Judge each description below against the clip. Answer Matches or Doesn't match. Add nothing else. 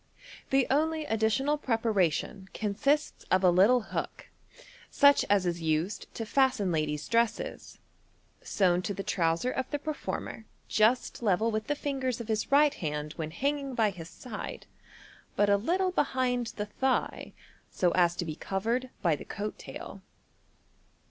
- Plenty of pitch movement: Matches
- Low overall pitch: Doesn't match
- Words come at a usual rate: Matches